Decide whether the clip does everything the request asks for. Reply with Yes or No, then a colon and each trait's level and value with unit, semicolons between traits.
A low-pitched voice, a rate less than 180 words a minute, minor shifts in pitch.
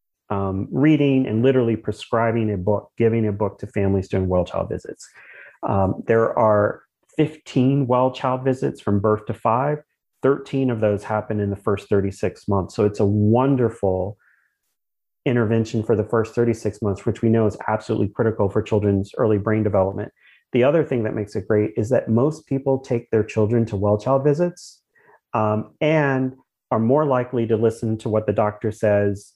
No: low, 110 Hz; average, 170 wpm; average, 3.4 semitones